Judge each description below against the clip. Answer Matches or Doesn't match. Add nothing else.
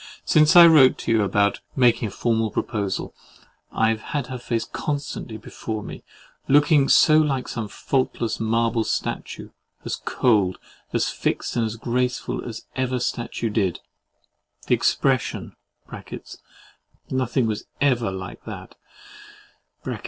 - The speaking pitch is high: Doesn't match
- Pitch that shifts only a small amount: Doesn't match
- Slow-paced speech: Matches